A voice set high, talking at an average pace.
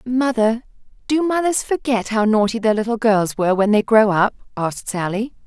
Yes: high, 225 Hz; average, 175 wpm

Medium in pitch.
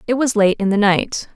No: high, 215 Hz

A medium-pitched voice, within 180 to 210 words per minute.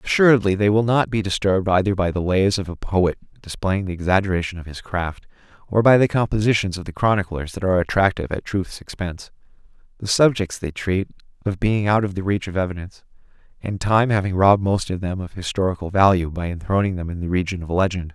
No: very low, 95 Hz; fast, 205 wpm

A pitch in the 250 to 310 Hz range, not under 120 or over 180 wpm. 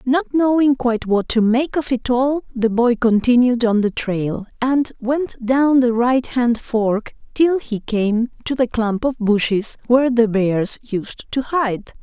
No: high, 240 Hz; average, 175 wpm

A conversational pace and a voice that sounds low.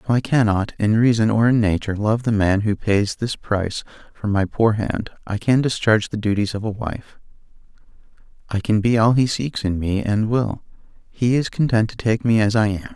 No: fast, 215 wpm; low, 110 Hz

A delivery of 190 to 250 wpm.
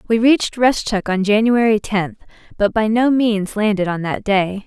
No: average, 180 wpm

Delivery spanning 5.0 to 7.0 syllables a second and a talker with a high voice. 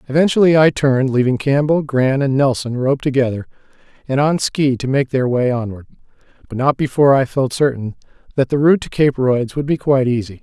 No: 5.9 syllables/s; low, 135 Hz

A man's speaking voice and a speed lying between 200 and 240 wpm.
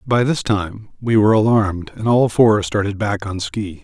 Yes: male; fast, 205 wpm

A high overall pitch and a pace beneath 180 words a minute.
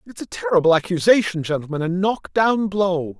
No: medium, 180 Hz; average, 170 wpm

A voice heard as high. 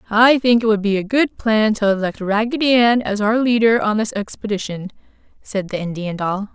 Yes: high, 215 Hz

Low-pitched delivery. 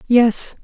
No: high, 235 Hz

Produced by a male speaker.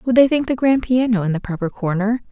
No: female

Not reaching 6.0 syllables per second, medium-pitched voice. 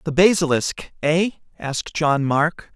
Yes: 4.0 syllables/s; medium, 160 Hz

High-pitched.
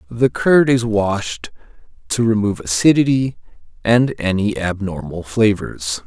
No: low, 105 Hz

